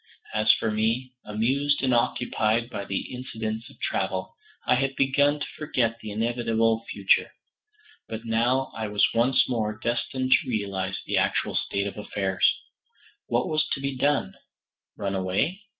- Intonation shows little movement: No, average, 3.5 semitones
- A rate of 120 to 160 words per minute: Yes, average, 150 wpm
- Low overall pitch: Yes, low, 115 Hz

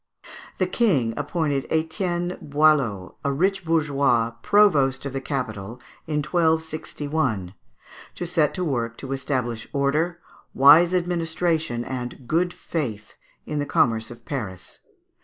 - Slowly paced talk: Yes, slow, 120 wpm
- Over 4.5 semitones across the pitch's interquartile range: Yes, average, 5.0 semitones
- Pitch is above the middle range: No, medium, 145 Hz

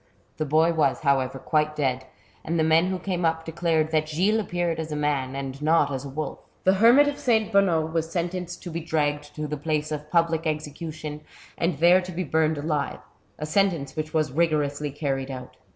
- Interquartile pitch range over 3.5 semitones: No, narrow, 2.5 semitones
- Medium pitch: Yes, medium, 155 Hz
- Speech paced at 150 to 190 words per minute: No, average, 200 wpm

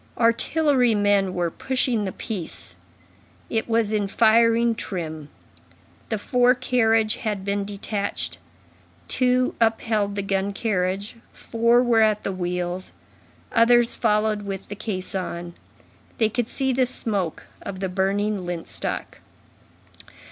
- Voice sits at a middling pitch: No, high, 210 Hz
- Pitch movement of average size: Yes, average, 3.2 semitones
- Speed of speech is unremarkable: No, slow, 125 wpm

